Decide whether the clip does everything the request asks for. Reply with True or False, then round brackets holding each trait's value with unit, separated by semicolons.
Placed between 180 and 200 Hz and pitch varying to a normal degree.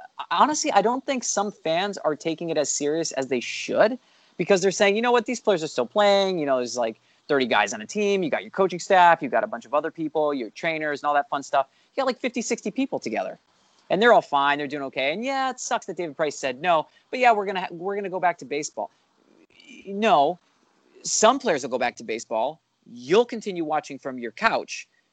False (190 Hz; 7.9 semitones)